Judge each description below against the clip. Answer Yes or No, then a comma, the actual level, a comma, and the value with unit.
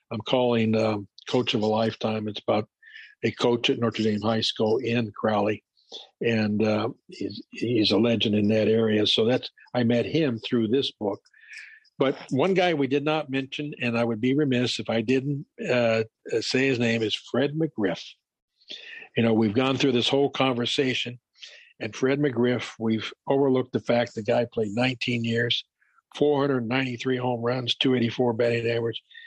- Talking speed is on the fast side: No, average, 170 wpm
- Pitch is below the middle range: Yes, low, 120 Hz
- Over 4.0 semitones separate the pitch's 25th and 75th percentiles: No, average, 3.0 semitones